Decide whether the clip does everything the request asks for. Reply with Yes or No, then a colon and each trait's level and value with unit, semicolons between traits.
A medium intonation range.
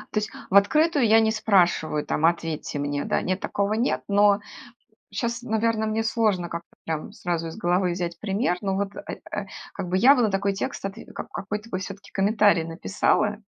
Yes: average, 3.7 semitones